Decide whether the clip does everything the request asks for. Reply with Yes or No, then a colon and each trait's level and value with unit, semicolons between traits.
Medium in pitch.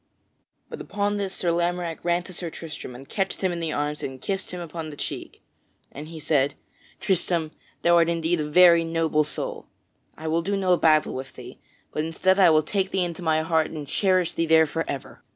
Yes: medium, 165 Hz